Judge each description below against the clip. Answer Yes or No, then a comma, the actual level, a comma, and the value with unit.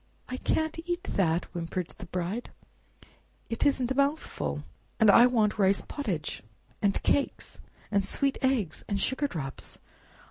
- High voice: Yes, high, 215 Hz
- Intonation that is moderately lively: No, wide, 7.0 semitones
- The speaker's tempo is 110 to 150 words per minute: Yes, average, 140 wpm